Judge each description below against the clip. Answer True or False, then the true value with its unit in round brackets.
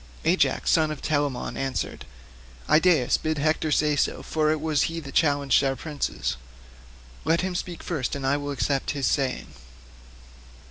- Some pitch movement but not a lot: False (2.2 semitones)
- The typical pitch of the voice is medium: True (150 Hz)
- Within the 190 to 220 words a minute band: False (155 wpm)